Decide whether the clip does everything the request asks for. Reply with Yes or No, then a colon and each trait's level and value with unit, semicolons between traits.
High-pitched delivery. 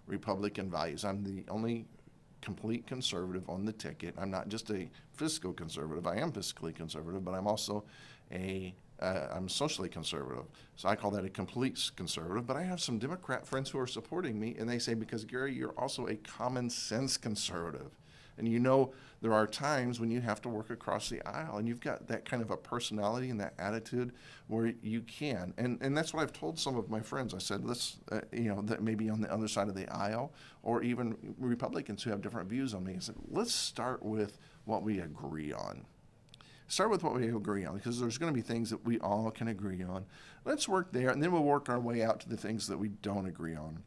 No: low, 115 Hz